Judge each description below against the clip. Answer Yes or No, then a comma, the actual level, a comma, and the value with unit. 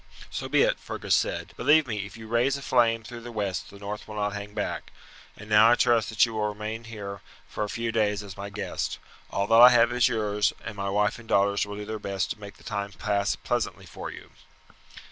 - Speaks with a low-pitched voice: Yes, low, 105 Hz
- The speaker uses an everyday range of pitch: No, narrow, 2.2 semitones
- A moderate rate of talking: No, fast, 240 wpm